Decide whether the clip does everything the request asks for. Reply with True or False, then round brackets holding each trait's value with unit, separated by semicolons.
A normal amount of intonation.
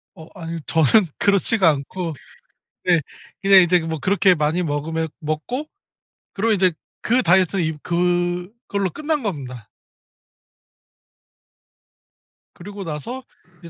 True (3.7 semitones)